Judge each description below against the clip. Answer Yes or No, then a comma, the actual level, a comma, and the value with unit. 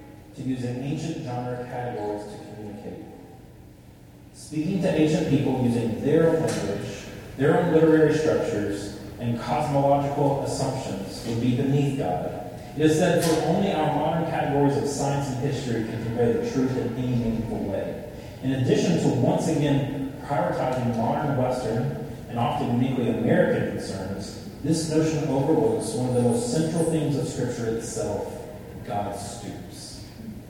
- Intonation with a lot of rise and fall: No, average, 4.9 semitones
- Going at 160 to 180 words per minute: No, average, 145 wpm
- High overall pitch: No, low, 130 Hz